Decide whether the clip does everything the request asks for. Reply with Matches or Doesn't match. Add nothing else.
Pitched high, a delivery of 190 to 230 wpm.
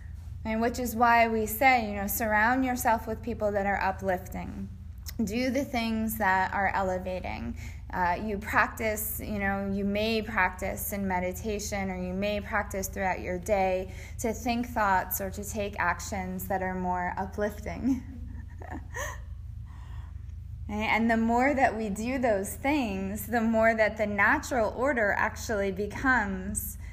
Doesn't match